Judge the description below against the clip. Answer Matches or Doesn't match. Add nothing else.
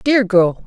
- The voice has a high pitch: Matches